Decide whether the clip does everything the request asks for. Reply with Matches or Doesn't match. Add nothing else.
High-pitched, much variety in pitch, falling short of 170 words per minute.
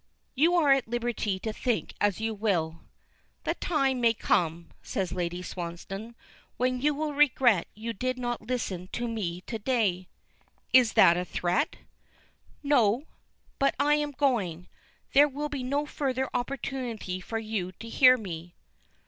Matches